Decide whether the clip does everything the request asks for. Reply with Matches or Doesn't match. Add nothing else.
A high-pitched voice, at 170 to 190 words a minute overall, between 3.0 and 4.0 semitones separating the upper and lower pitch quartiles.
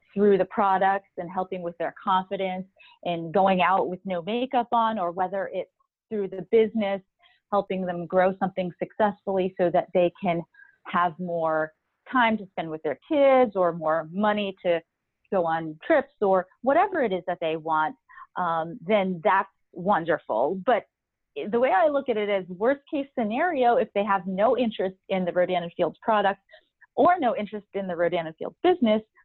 Doesn't match